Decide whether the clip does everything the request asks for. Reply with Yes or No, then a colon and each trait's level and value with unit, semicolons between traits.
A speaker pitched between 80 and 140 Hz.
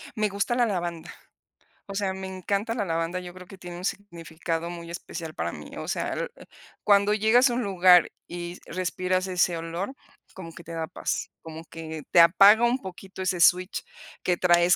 No: medium, 180 Hz